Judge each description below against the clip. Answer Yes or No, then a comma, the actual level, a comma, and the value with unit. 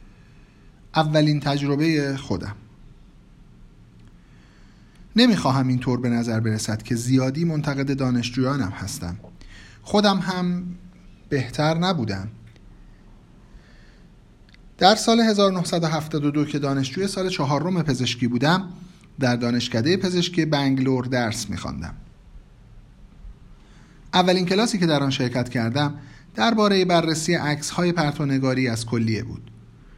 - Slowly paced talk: Yes, slow, 90 wpm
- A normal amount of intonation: No, wide, 6.4 semitones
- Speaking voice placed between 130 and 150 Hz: Yes, medium, 140 Hz